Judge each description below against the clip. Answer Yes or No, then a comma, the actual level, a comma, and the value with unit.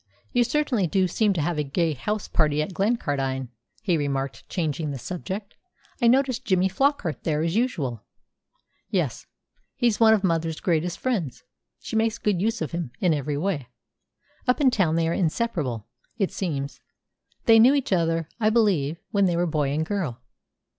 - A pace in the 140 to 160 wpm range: No, average, 175 wpm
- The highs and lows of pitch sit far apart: Yes, wide, 6.3 semitones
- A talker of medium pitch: Yes, medium, 175 Hz